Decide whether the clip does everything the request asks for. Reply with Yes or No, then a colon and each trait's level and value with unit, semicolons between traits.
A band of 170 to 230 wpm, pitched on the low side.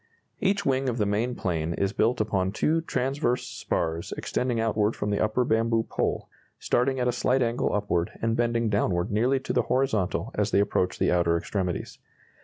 Yes: average, 185 wpm; low, 115 Hz